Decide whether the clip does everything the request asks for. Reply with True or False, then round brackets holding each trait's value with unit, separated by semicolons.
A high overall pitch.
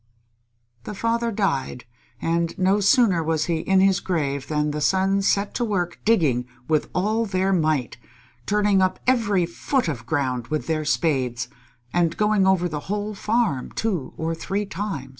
False (180 Hz)